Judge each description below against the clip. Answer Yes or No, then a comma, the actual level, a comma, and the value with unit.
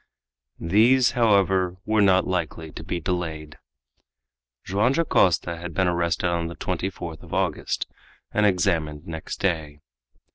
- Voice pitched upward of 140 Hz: No, very low, 90 Hz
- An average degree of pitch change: Yes, average, 3.0 semitones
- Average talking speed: No, slow, 130 wpm